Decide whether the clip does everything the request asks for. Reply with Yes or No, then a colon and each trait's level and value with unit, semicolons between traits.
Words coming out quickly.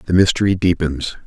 No: average, 140 wpm